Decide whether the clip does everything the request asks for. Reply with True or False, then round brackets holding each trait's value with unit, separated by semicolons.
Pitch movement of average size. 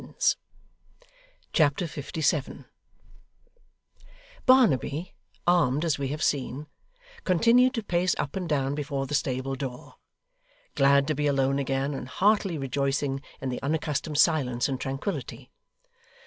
True (3.5 semitones)